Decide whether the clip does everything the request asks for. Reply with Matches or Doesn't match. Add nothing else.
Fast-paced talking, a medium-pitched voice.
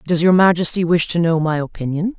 Matches